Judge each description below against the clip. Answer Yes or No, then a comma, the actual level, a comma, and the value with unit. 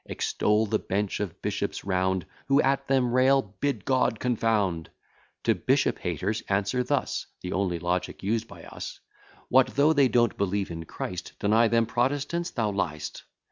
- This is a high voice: No, low, 110 Hz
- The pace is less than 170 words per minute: Yes, average, 150 wpm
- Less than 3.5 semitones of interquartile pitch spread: No, average, 5.0 semitones